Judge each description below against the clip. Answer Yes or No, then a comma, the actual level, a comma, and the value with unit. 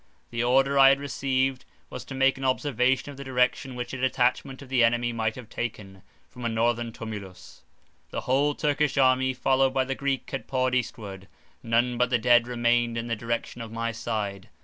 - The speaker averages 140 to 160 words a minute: No, average, 195 wpm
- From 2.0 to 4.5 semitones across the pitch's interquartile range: Yes, narrow, 2.4 semitones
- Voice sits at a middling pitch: No, low, 125 Hz